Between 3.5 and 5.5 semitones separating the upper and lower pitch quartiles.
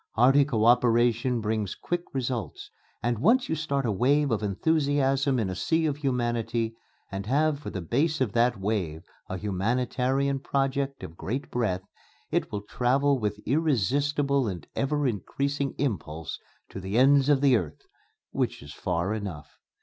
Yes: average, 5.1 semitones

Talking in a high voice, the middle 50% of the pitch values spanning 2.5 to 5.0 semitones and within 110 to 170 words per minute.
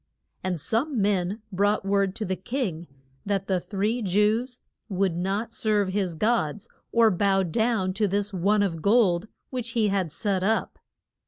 Yes: high, 200 Hz; average, 2.8 semitones; average, 160 wpm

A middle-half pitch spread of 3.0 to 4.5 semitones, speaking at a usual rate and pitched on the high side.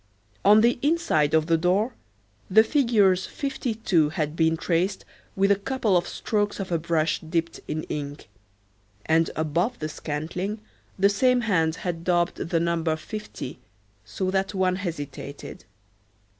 No: average, 4.2 semitones; average, 145 wpm; medium, 180 Hz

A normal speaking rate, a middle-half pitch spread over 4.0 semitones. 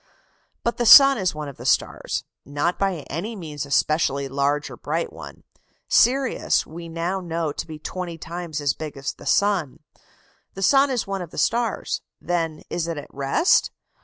Yes: average, 185 wpm; average, 4.8 semitones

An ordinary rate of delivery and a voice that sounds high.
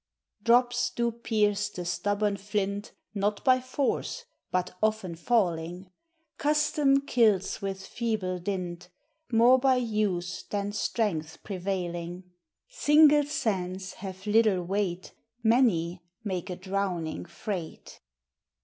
No: slow, 105 wpm; high, 200 Hz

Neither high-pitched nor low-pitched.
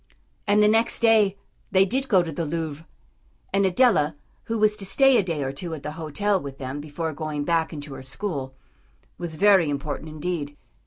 Yes: medium, 165 Hz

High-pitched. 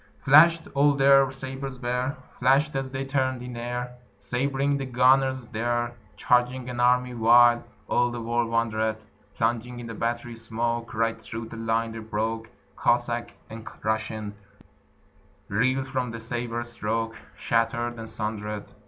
No: low, 120 Hz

